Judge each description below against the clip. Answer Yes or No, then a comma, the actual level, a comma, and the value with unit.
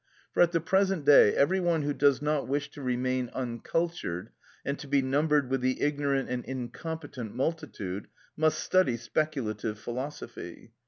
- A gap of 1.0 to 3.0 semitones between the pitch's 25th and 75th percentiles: No, average, 3.7 semitones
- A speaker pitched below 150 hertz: Yes, medium, 140 Hz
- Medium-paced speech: Yes, average, 155 wpm